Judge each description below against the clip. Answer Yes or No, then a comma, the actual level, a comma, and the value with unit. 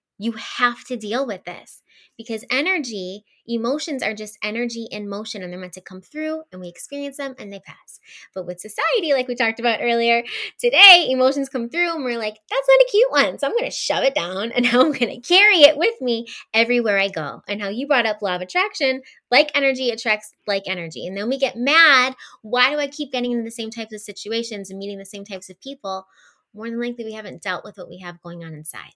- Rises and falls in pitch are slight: No, average, 5.1 semitones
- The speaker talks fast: Yes, fast, 235 wpm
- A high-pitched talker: Yes, high, 230 Hz